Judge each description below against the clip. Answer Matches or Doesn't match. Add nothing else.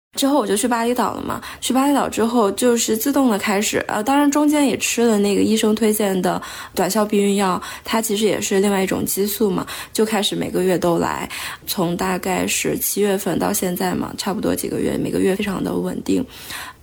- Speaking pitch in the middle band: Doesn't match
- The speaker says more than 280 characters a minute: Matches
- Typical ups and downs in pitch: Matches